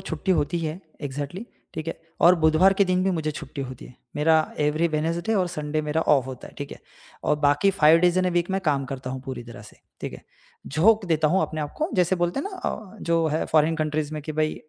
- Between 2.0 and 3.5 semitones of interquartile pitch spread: Yes, average, 3.2 semitones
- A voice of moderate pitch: Yes, medium, 155 Hz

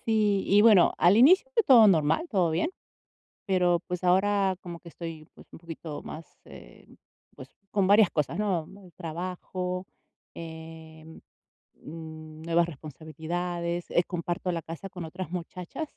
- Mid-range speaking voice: Yes, medium, 175 Hz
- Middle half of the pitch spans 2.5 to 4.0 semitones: Yes, average, 2.9 semitones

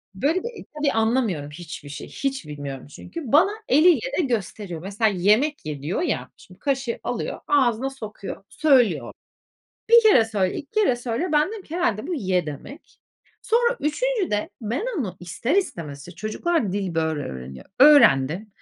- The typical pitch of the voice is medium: No, high, 230 Hz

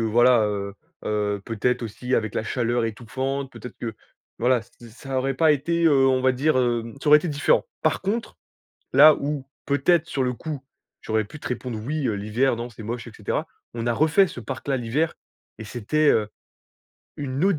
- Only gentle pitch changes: No, average, 4.2 semitones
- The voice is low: Yes, low, 125 Hz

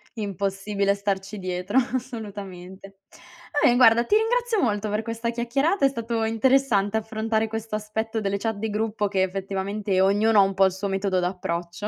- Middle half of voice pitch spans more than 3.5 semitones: No, narrow, 2.6 semitones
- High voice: Yes, high, 210 Hz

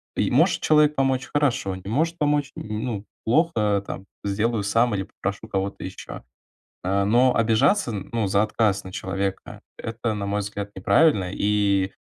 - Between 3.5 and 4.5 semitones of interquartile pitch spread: Yes, average, 3.9 semitones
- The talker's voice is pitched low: Yes, low, 105 Hz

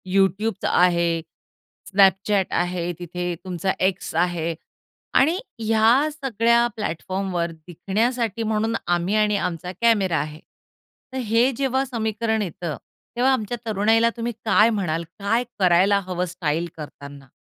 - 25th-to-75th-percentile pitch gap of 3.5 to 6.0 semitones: Yes, average, 4.4 semitones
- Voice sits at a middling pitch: No, high, 200 Hz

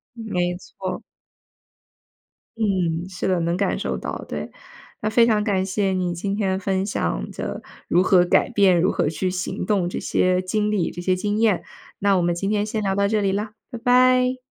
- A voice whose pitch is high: Yes, high, 195 Hz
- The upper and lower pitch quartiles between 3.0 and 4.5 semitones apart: No, narrow, 2.6 semitones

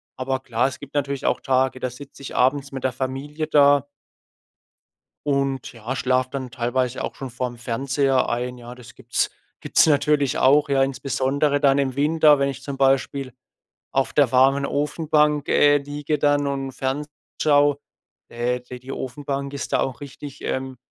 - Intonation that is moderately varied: No, narrow, 1.9 semitones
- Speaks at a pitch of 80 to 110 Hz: No, low, 135 Hz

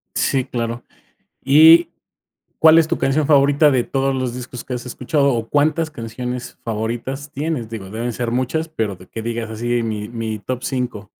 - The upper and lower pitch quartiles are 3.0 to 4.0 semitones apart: Yes, average, 3.7 semitones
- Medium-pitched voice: No, low, 125 Hz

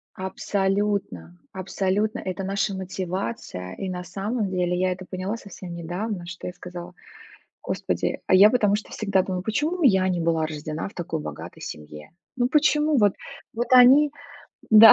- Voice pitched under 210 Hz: Yes, high, 190 Hz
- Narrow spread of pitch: No, average, 3.3 semitones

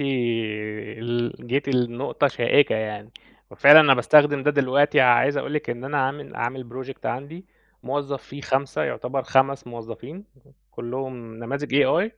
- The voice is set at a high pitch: No, low, 130 Hz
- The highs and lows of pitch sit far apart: No, average, 3.1 semitones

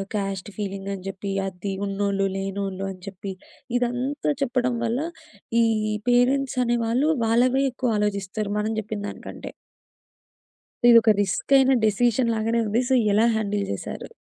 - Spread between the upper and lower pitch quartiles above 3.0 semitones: Yes, average, 3.7 semitones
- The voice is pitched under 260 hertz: Yes, high, 215 Hz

